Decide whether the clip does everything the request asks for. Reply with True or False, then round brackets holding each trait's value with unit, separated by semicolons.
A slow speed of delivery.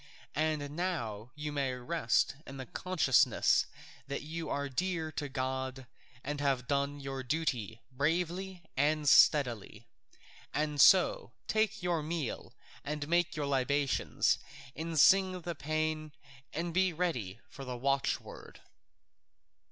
True (125 wpm)